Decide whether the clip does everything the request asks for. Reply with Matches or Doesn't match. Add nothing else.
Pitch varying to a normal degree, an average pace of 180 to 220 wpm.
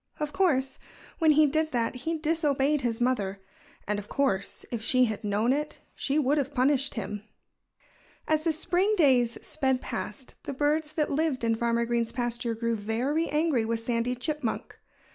Doesn't match